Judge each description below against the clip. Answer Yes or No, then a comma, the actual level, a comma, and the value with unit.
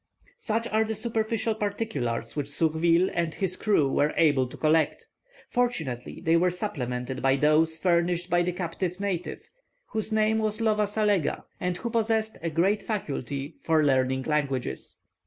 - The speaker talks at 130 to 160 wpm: Yes, average, 155 wpm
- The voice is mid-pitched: Yes, medium, 175 Hz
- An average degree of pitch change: No, wide, 6.2 semitones